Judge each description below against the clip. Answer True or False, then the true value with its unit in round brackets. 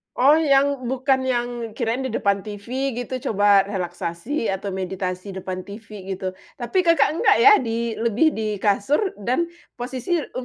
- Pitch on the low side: False (230 Hz)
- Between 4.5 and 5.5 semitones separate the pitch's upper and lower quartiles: True (5.0 semitones)